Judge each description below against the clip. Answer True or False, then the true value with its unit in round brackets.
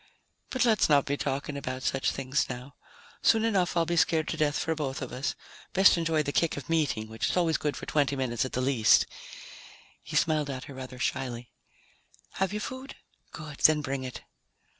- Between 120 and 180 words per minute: False (200 wpm)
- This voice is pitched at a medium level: True (145 Hz)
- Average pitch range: True (4.0 semitones)